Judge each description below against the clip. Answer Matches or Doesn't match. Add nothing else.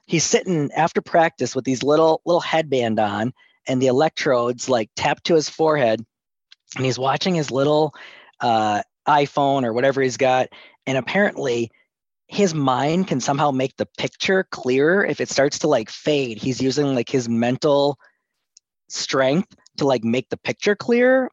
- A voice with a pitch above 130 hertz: Matches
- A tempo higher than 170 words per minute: Doesn't match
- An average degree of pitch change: Matches